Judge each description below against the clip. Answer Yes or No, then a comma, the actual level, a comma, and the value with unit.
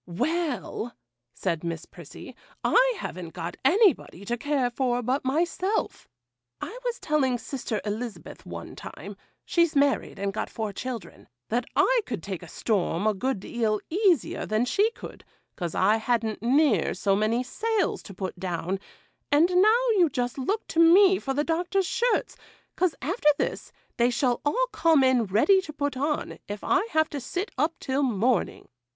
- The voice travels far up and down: Yes, wide, 7.6 semitones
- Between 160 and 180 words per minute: Yes, average, 165 wpm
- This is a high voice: Yes, very high, 260 Hz